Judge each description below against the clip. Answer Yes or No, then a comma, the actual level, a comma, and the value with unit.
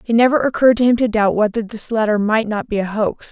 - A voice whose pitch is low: No, high, 220 Hz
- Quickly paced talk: Yes, fast, 270 wpm